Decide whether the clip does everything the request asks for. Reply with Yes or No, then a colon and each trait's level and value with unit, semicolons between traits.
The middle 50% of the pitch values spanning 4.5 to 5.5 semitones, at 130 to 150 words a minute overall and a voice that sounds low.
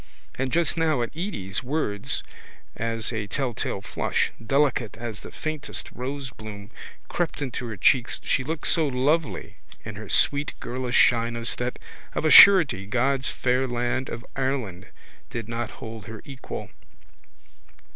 No: average, 3.7 semitones; average, 140 wpm; low, 125 Hz